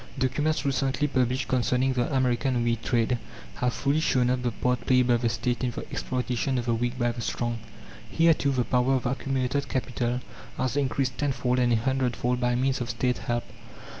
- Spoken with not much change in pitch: Yes, narrow, 1.6 semitones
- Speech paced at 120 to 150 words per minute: No, average, 195 wpm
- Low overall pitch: Yes, low, 125 Hz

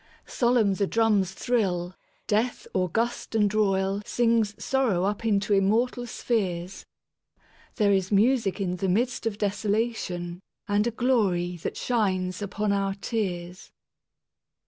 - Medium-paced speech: No, slow, 110 wpm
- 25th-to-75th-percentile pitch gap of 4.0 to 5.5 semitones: No, average, 3.1 semitones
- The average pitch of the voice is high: Yes, high, 205 Hz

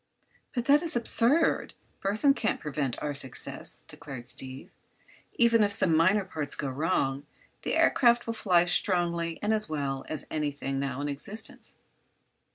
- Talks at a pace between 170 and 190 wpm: No, average, 155 wpm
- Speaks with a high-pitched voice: No, medium, 170 Hz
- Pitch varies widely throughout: Yes, wide, 7.6 semitones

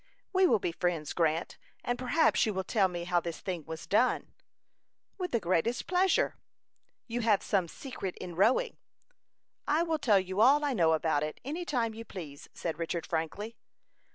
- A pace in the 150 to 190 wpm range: Yes, average, 180 wpm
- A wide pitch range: Yes, wide, 6.9 semitones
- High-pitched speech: Yes, high, 195 Hz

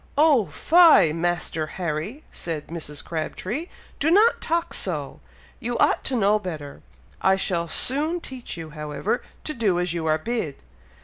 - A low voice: No, medium, 185 Hz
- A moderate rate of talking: Yes, average, 150 wpm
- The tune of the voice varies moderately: No, wide, 8.9 semitones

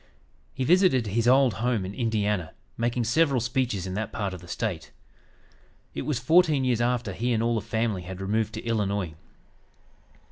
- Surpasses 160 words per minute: Yes, average, 175 wpm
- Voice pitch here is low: Yes, low, 115 Hz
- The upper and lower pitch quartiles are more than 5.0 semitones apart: No, average, 3.5 semitones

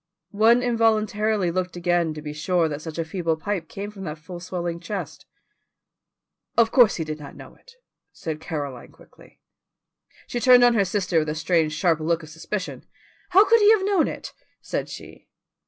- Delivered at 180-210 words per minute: Yes, average, 185 wpm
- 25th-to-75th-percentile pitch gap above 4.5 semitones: Yes, average, 5.2 semitones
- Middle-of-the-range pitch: Yes, medium, 180 Hz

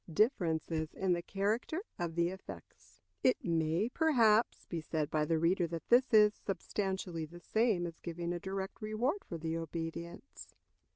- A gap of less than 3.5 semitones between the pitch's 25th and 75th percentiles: No, average, 4.5 semitones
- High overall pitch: No, medium, 175 Hz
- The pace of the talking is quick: No, average, 160 wpm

